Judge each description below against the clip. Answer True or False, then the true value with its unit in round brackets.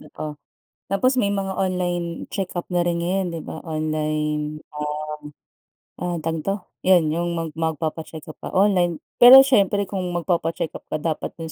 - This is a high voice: False (170 Hz)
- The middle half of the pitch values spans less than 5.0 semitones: True (3.3 semitones)